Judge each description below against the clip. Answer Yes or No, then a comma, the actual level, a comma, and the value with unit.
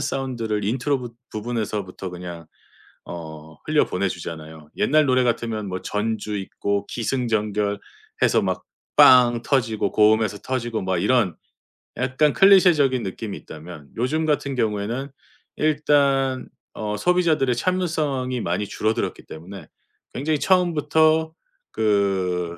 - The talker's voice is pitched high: No, low, 115 Hz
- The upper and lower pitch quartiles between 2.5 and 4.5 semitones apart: No, wide, 5.6 semitones